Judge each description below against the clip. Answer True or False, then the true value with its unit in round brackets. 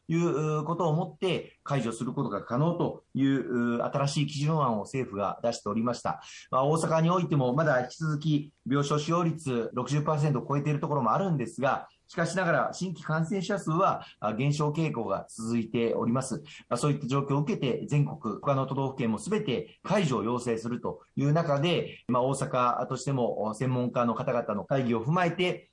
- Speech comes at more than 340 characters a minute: True (365 characters per minute)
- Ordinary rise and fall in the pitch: True (4.4 semitones)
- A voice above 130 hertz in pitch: True (140 Hz)